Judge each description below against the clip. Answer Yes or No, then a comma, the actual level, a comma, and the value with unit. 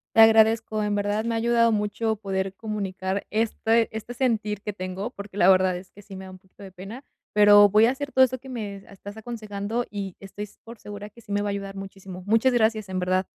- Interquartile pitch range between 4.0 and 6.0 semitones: No, narrow, 2.4 semitones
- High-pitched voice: Yes, high, 205 Hz